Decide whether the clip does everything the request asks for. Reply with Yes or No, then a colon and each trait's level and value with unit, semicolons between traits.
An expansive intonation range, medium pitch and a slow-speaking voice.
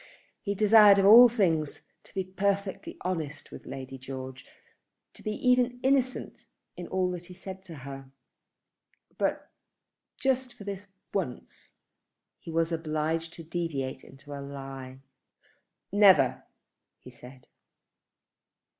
Yes: wide, 6.6 semitones; medium, 170 Hz; slow, 125 wpm